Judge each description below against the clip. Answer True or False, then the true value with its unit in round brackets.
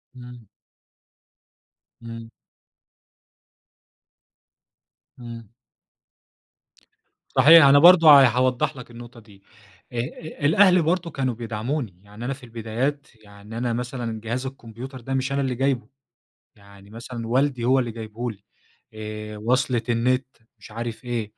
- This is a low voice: True (120 Hz)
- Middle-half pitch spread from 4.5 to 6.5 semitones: False (2.9 semitones)